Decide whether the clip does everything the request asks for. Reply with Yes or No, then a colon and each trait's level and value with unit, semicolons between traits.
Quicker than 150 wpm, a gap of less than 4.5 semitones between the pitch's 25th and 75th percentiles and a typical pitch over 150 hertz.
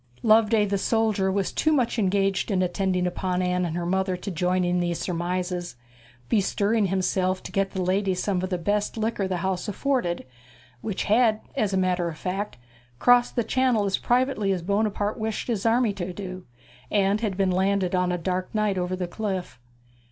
Yes: average, 190 wpm; average, 2.7 semitones; high, 190 Hz